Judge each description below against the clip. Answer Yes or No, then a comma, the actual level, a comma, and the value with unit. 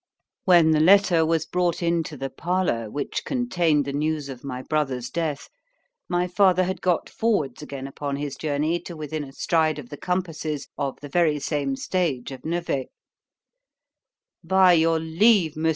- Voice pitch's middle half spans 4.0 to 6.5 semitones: No, average, 3.6 semitones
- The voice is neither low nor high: Yes, medium, 160 Hz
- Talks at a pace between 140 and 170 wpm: Yes, average, 160 wpm